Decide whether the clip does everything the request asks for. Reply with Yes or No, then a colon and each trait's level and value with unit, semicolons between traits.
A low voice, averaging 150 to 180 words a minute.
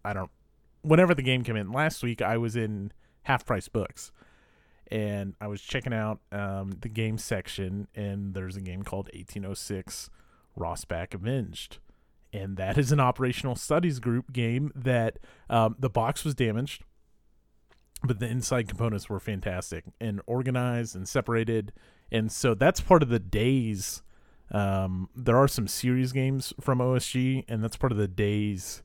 Yes: low, 115 Hz; average, 160 wpm